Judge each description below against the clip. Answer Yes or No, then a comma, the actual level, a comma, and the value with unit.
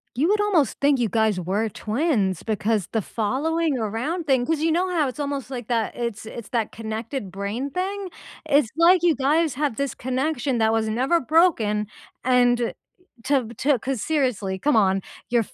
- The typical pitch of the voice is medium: No, very high, 250 Hz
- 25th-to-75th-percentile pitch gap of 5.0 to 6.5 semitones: Yes, wide, 5.4 semitones